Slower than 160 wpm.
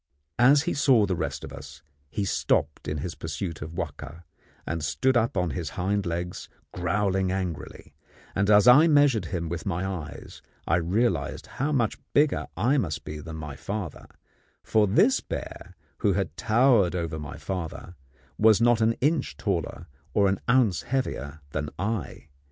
No: average, 165 wpm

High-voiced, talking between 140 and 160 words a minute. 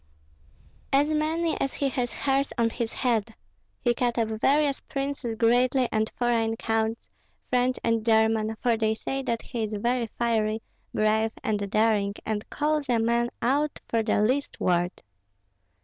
Yes: high, 235 Hz; average, 155 wpm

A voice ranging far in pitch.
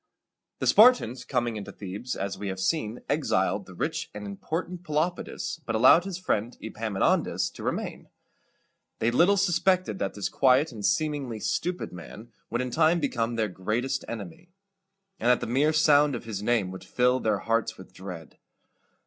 Yes: wide, 6.9 semitones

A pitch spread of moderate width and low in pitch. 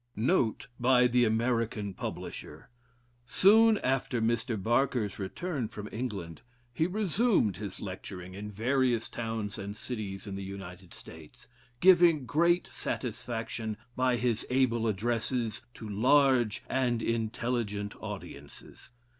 Yes: average, 3.7 semitones; low, 115 Hz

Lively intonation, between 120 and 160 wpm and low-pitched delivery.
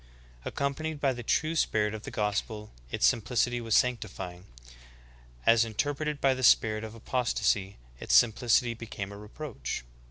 No: average, 3.6 semitones; average, 140 wpm; low, 115 Hz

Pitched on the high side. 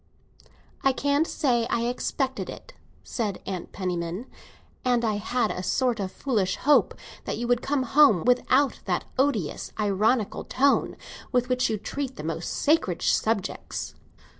Yes: high, 240 Hz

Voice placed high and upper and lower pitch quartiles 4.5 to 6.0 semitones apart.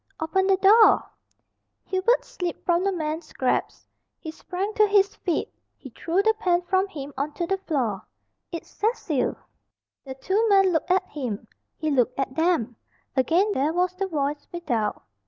Yes: very high, 345 Hz; average, 5.1 semitones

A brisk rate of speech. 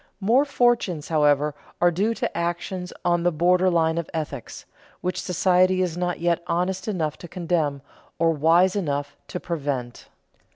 No: average, 155 wpm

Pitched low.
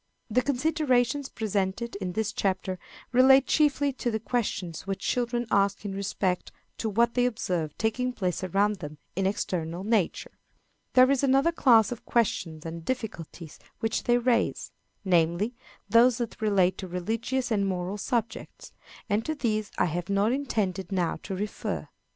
No: high, 215 Hz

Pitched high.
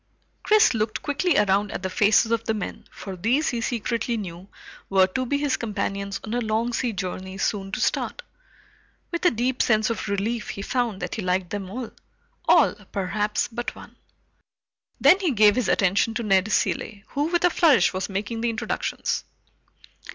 Yes: high, 220 Hz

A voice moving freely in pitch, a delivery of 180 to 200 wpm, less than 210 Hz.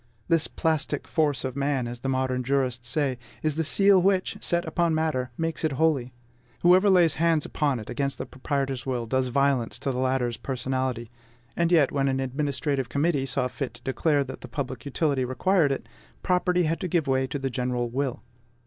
No: average, 3.6 semitones; average, 190 wpm; medium, 140 Hz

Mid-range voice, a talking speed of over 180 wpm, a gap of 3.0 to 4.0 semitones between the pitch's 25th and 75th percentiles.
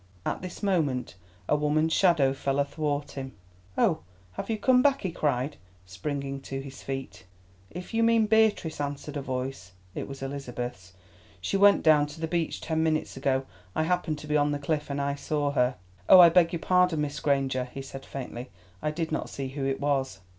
Yes: medium, 145 Hz; average, 190 wpm; average, 3.3 semitones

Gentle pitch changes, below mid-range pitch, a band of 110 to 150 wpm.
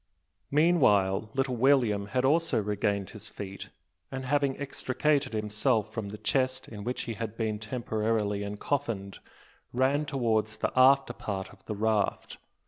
No: average, 4.3 semitones; low, 115 Hz; average, 140 wpm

